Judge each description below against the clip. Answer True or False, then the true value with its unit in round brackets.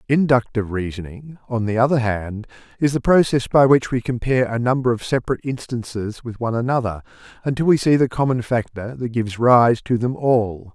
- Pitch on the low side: True (120 Hz)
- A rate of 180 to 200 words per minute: True (185 wpm)